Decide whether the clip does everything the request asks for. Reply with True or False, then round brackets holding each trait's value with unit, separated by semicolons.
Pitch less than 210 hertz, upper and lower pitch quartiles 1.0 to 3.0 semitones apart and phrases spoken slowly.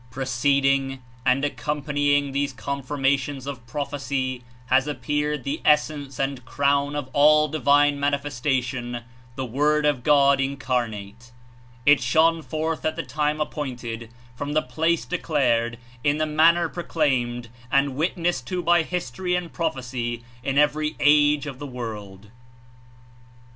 True (140 Hz; 2.7 semitones; 130 wpm)